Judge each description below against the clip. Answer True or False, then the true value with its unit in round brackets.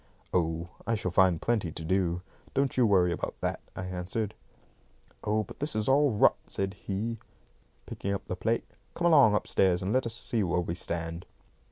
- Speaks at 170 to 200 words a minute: True (185 wpm)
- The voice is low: True (95 Hz)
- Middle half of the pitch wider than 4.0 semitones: True (4.4 semitones)